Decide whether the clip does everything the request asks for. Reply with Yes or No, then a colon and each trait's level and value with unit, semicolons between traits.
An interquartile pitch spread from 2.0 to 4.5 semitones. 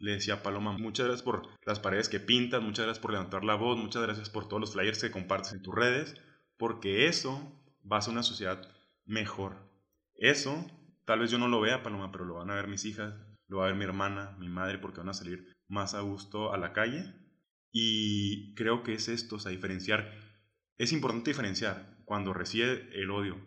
Yes: average, 2.9 semitones